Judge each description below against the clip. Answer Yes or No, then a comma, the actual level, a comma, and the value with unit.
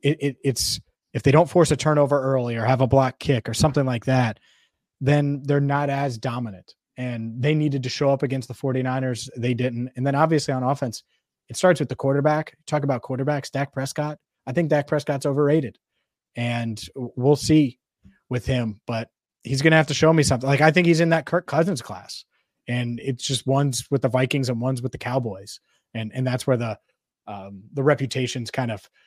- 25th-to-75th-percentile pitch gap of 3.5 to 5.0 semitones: No, average, 2.8 semitones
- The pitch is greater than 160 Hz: No, low, 135 Hz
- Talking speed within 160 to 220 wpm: Yes, fast, 205 wpm